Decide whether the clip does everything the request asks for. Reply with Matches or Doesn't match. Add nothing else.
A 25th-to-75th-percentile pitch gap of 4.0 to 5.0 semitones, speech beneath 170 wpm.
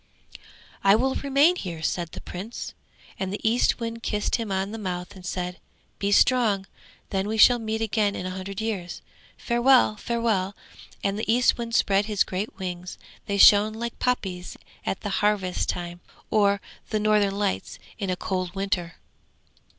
Doesn't match